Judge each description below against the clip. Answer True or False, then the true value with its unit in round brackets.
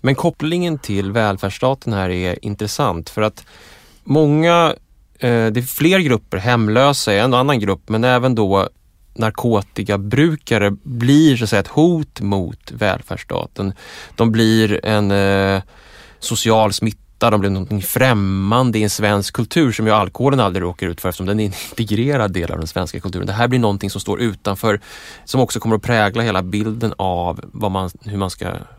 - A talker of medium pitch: False (110 Hz)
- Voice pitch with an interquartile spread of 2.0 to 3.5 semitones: False (3.9 semitones)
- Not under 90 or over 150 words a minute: False (170 wpm)